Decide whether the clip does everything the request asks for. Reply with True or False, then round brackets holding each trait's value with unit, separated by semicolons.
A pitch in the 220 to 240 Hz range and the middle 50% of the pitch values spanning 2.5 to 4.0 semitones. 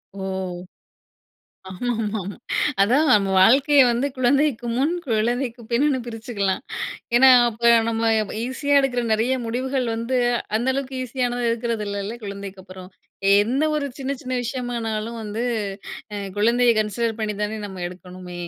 True (235 Hz; 3.3 semitones)